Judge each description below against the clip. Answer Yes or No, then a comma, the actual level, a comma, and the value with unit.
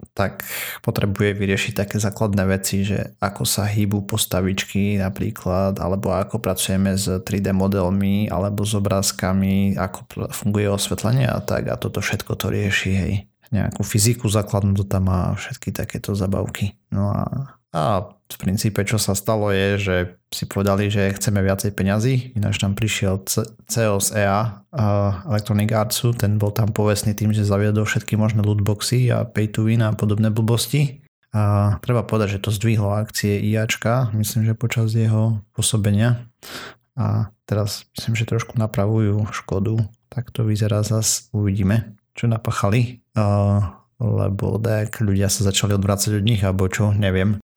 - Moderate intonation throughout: No, narrow, 1.9 semitones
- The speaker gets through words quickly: No, average, 155 wpm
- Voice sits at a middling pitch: No, low, 105 Hz